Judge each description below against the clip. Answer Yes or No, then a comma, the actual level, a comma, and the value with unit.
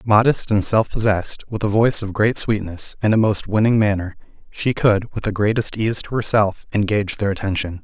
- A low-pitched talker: Yes, low, 105 Hz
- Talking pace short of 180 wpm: No, average, 200 wpm